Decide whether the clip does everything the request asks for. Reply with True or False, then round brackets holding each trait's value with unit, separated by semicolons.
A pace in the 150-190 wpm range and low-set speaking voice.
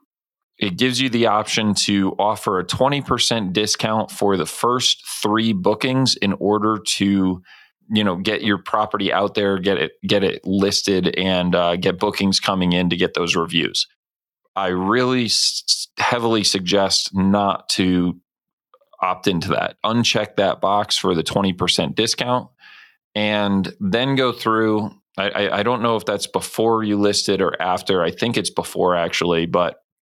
True (160 wpm; 100 Hz)